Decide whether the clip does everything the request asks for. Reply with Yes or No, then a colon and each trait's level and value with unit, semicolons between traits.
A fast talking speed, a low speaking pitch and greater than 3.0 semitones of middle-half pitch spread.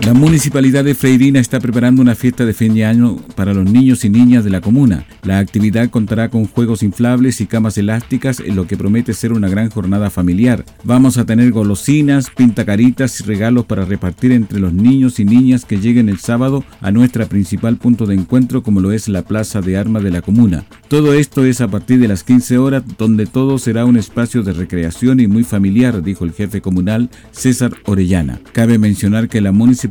Yes: fast, 205 wpm; low, 115 Hz; average, 3.6 semitones